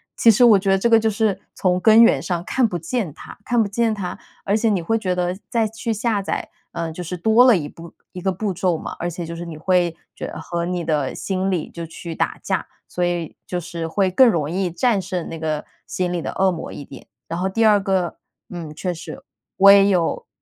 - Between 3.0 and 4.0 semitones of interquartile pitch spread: Yes, average, 3.7 semitones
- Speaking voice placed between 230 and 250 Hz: No, medium, 185 Hz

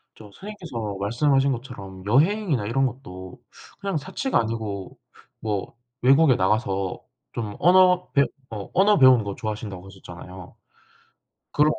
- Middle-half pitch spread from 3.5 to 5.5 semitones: No, wide, 6.9 semitones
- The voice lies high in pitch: No, low, 115 Hz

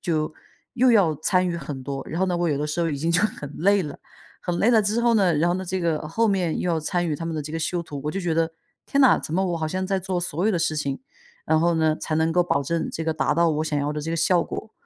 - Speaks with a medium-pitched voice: Yes, medium, 170 Hz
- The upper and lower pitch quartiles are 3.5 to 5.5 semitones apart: No, average, 3.1 semitones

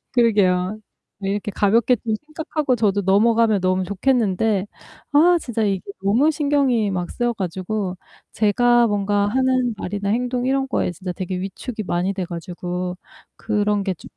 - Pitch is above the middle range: Yes, high, 205 Hz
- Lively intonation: No, average, 4.3 semitones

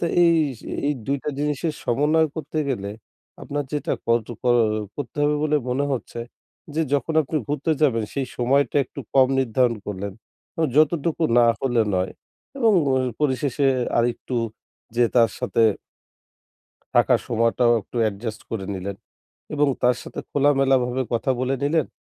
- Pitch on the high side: No, low, 130 Hz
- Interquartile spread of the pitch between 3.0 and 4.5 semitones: Yes, average, 3.9 semitones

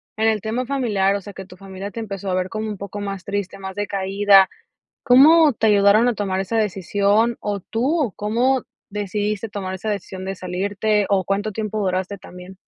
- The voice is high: Yes, high, 205 Hz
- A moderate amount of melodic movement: No, narrow, 2.2 semitones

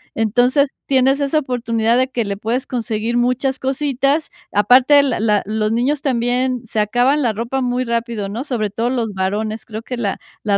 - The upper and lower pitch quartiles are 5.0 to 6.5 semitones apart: No, average, 3.2 semitones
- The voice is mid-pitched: No, high, 240 Hz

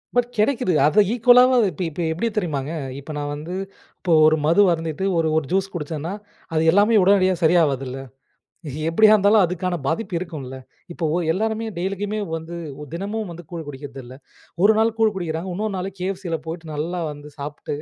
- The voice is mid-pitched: Yes, medium, 175 Hz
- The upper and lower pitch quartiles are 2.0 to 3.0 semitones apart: No, average, 4.6 semitones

